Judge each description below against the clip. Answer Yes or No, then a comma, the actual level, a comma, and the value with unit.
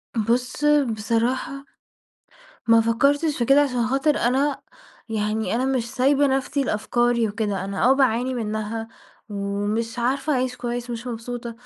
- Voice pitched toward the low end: No, high, 240 Hz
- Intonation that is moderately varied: Yes, average, 3.1 semitones